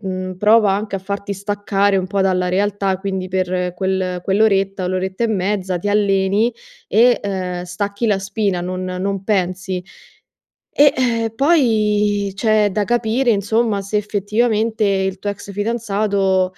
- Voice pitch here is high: Yes, high, 200 Hz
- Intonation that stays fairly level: Yes, narrow, 2.1 semitones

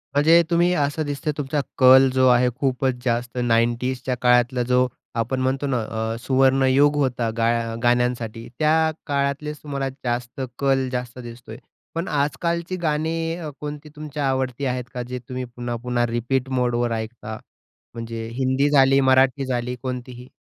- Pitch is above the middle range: No, low, 130 Hz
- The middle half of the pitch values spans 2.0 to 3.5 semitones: Yes, average, 2.7 semitones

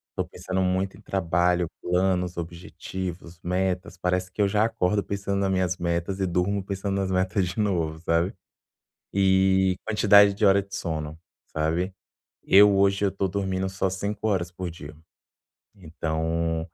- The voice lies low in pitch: Yes, very low, 95 Hz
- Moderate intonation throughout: No, narrow, 2.0 semitones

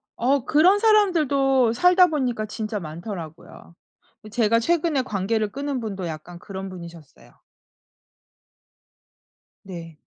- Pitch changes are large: Yes, wide, 7.3 semitones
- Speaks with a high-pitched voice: Yes, high, 225 Hz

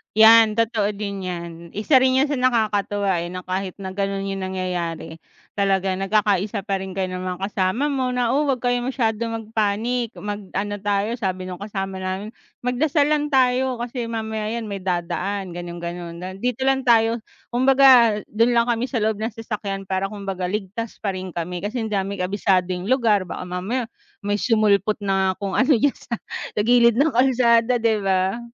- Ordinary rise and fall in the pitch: Yes, average, 3.9 semitones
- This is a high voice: Yes, high, 210 Hz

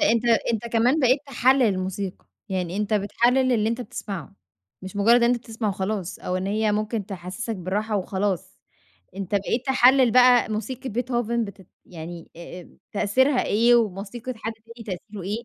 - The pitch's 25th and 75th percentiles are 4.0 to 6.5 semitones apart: No, average, 3.6 semitones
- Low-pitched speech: No, high, 220 Hz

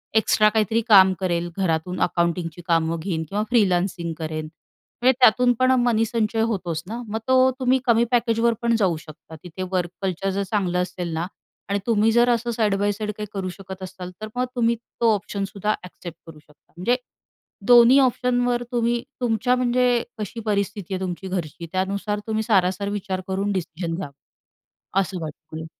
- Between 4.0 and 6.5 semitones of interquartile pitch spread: Yes, average, 4.4 semitones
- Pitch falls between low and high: No, high, 200 Hz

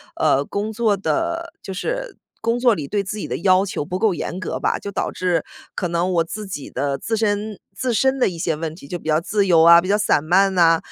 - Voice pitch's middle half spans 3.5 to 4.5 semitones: Yes, average, 4.2 semitones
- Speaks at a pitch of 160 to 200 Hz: Yes, high, 190 Hz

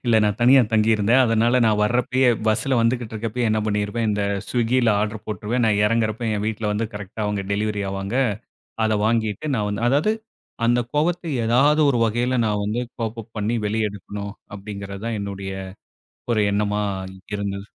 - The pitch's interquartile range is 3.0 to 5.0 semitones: No, narrow, 2.5 semitones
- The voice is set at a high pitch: No, low, 110 Hz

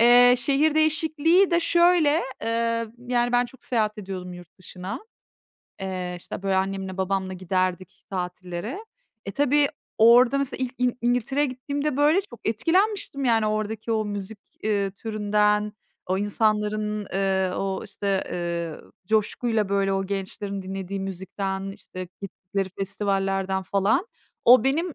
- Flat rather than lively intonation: No, average, 4.5 semitones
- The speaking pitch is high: Yes, high, 210 Hz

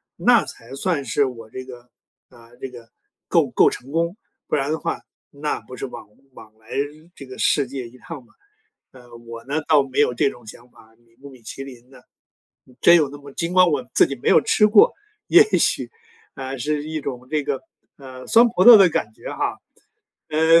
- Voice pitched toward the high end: No, low, 135 Hz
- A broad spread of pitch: No, average, 4.0 semitones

